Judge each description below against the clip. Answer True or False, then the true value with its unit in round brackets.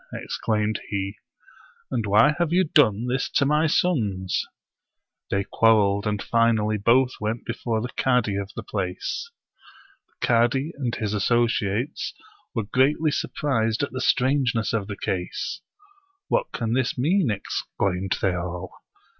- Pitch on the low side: True (115 Hz)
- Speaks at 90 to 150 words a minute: True (145 wpm)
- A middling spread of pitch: True (4.5 semitones)